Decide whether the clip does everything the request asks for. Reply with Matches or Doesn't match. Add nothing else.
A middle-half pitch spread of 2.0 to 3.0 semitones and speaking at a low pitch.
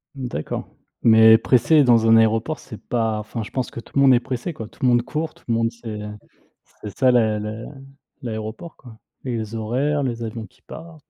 Matches